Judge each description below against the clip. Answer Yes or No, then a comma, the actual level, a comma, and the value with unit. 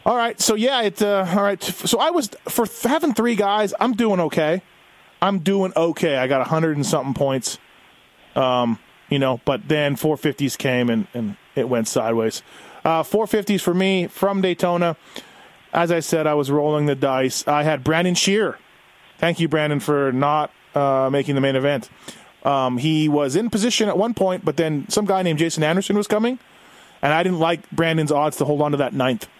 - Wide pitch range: Yes, wide, 5.7 semitones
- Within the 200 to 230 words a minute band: Yes, fast, 205 wpm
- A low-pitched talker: No, medium, 160 Hz